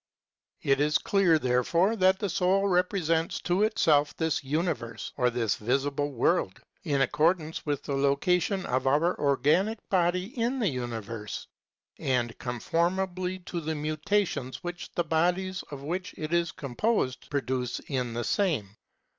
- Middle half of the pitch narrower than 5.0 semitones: No, wide, 5.4 semitones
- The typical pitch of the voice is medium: Yes, medium, 155 Hz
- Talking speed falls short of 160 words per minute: Yes, average, 145 wpm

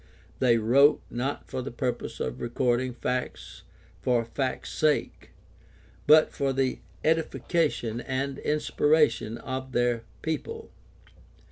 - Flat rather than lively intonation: No, average, 3.3 semitones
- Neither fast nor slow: No, slow, 110 wpm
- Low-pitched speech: Yes, low, 130 Hz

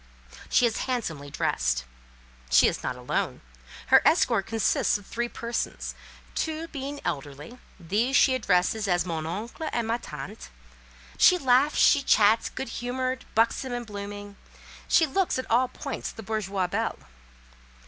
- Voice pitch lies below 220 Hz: No, high, 225 Hz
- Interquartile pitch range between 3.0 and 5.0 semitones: No, wide, 5.4 semitones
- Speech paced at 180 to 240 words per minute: No, average, 140 wpm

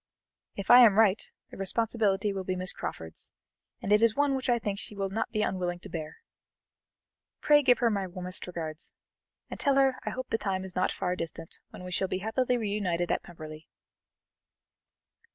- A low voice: No, high, 195 Hz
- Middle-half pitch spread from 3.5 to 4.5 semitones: Yes, average, 3.9 semitones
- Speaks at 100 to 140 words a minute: No, average, 190 wpm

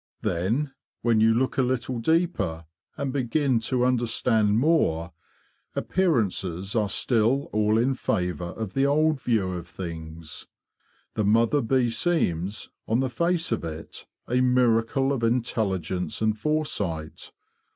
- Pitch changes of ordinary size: No, wide, 5.7 semitones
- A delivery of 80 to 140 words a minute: Yes, slow, 135 wpm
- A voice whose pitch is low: Yes, low, 115 Hz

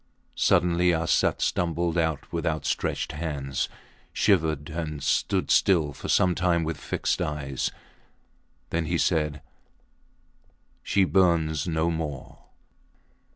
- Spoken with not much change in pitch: Yes, narrow, 2.2 semitones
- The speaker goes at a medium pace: No, slow, 110 wpm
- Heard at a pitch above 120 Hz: No, very low, 80 Hz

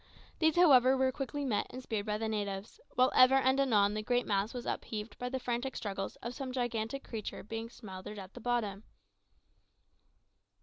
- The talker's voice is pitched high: Yes, high, 240 Hz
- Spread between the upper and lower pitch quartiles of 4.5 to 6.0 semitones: No, average, 3.6 semitones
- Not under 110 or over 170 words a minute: No, average, 190 wpm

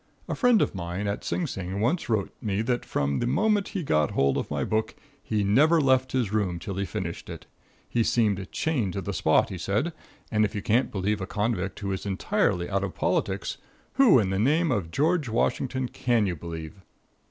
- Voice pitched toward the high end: No, low, 105 Hz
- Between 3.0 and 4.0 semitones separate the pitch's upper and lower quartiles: No, average, 5.2 semitones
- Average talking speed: No, fast, 210 wpm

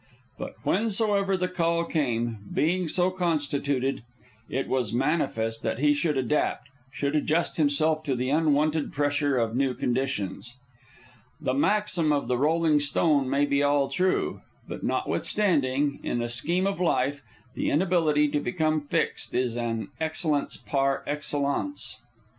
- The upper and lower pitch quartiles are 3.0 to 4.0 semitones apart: Yes, average, 3.7 semitones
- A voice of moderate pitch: Yes, medium, 145 Hz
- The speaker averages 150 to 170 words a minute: No, average, 140 wpm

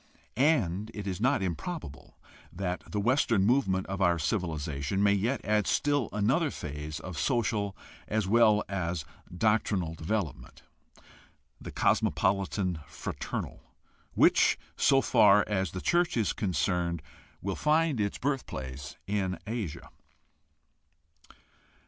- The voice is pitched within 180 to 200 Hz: No, low, 100 Hz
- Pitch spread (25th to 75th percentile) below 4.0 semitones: No, average, 4.4 semitones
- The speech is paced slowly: Yes, slow, 120 wpm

